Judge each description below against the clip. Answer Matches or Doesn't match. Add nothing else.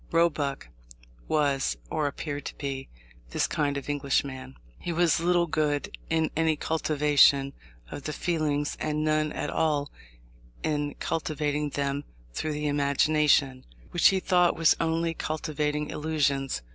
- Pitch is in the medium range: Matches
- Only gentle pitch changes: Matches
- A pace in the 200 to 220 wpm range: Doesn't match